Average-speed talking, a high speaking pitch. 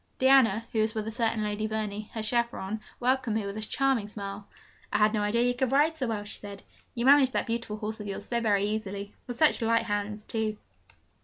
No: fast, 225 wpm; high, 220 Hz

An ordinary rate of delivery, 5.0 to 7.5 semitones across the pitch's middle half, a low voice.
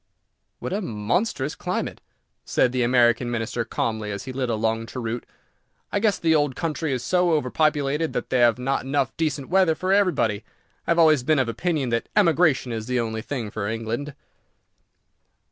Yes: average, 180 wpm; average, 5.3 semitones; low, 130 Hz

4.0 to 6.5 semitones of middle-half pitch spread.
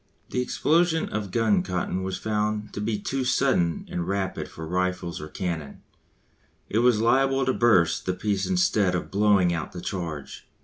Yes: average, 4.6 semitones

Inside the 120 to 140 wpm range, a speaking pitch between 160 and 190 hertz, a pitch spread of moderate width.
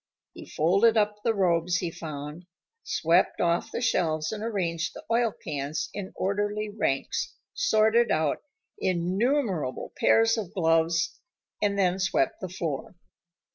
Yes: slow, 135 wpm; medium, 185 Hz; average, 4.3 semitones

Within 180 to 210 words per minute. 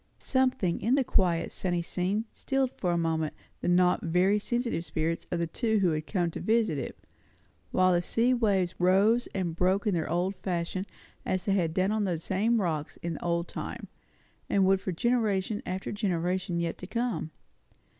Yes: average, 185 wpm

